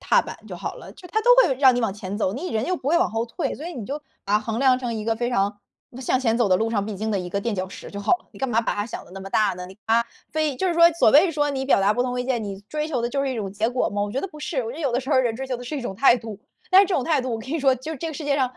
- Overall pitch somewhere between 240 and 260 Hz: Yes, high, 245 Hz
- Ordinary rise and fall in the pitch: Yes, average, 4.8 semitones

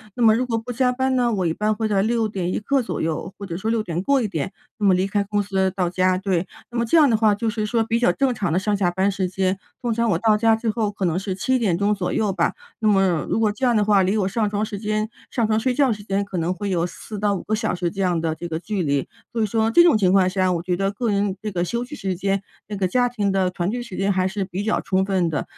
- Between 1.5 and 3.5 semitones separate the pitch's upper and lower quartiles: Yes, average, 3.2 semitones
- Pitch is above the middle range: Yes, high, 205 Hz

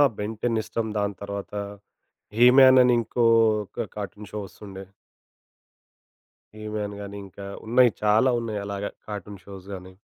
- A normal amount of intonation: No, narrow, 2.2 semitones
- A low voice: Yes, low, 105 Hz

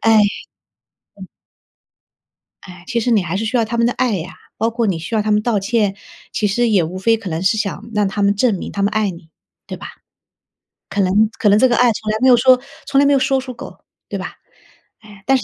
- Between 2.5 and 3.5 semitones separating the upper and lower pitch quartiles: Yes, average, 3.2 semitones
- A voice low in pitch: No, high, 215 Hz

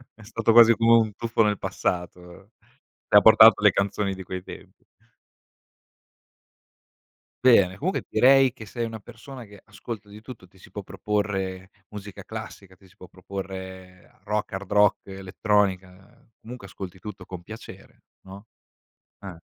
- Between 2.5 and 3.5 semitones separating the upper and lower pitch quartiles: Yes, average, 2.9 semitones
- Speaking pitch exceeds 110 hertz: No, low, 100 Hz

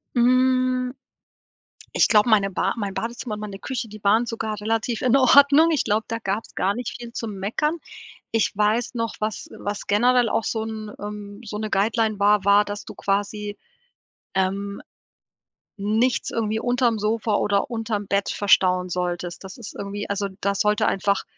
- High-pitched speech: Yes, high, 215 Hz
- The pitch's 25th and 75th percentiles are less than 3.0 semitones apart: Yes, narrow, 2.5 semitones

